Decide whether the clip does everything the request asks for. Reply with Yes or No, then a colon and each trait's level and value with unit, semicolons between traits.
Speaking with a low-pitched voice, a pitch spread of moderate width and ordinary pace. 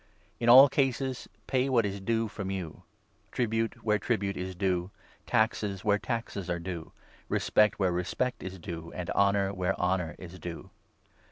Yes: low, 100 Hz; average, 3.9 semitones; average, 170 wpm